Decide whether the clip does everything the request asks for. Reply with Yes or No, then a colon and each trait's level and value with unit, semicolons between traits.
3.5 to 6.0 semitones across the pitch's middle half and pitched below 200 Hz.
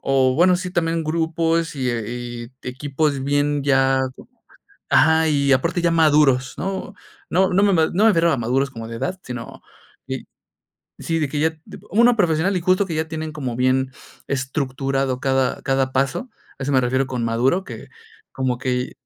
Yes: average, 4.1 semitones; medium, 140 Hz